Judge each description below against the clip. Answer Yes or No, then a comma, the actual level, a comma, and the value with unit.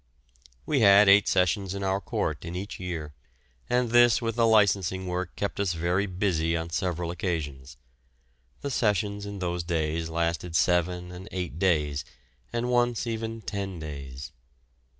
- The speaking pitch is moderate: No, very low, 90 Hz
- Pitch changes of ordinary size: Yes, average, 3.5 semitones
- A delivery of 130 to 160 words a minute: Yes, average, 150 wpm